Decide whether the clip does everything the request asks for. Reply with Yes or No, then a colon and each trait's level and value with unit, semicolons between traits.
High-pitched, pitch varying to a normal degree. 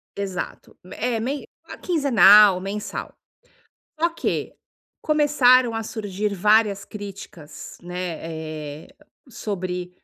Yes: high, 210 Hz; average, 4.8 semitones